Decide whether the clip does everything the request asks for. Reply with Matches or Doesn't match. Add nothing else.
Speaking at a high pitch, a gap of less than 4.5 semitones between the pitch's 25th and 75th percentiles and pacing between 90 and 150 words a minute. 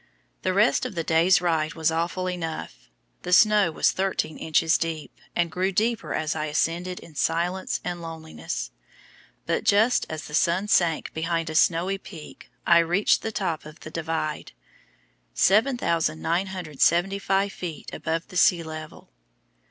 Doesn't match